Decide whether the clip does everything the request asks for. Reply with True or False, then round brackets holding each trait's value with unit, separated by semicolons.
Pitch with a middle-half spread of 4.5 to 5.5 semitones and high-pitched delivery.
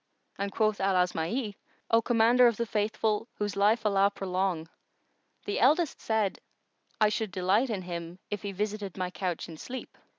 False (2.9 semitones; 205 Hz)